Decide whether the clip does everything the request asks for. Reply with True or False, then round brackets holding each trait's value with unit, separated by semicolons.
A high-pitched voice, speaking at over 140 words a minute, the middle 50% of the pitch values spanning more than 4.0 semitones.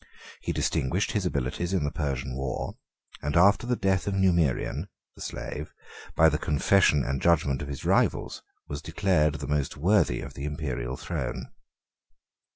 False (75 Hz; 160 wpm; 5.1 semitones)